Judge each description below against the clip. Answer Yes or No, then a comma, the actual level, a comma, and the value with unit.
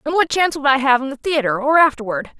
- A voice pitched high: Yes, very high, 275 Hz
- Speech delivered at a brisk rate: Yes, fast, 275 wpm